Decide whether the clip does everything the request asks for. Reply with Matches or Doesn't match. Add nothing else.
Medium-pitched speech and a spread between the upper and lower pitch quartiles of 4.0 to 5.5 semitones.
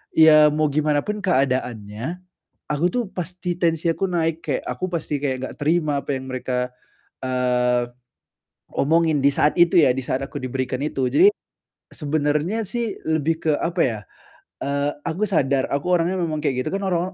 Matches